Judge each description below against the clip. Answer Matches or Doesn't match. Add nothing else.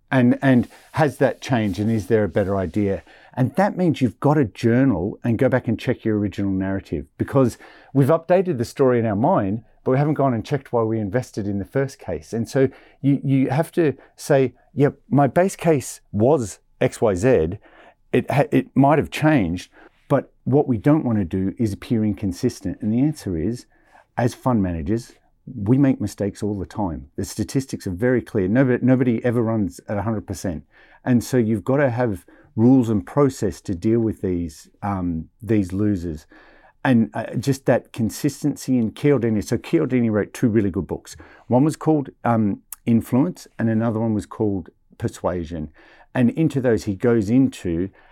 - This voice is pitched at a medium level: Doesn't match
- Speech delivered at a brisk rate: Doesn't match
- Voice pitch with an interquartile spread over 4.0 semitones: Matches